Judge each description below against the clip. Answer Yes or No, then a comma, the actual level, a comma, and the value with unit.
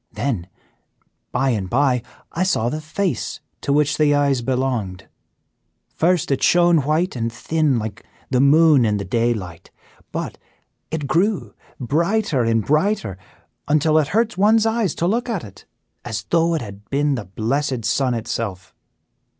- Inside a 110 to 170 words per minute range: Yes, average, 150 wpm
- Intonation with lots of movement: Yes, wide, 6.1 semitones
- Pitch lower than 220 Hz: Yes, medium, 140 Hz